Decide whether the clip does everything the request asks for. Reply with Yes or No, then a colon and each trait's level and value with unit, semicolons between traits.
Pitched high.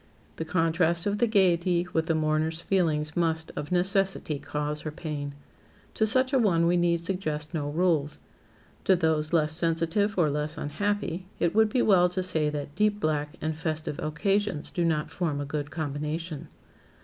No: medium, 165 Hz